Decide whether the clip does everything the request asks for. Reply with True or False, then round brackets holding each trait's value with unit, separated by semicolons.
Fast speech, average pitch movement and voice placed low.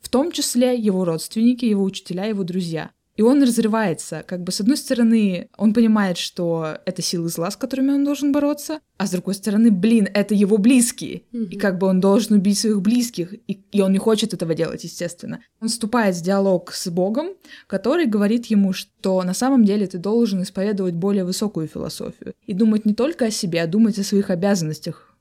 False (195 wpm; 3.7 semitones; 205 Hz)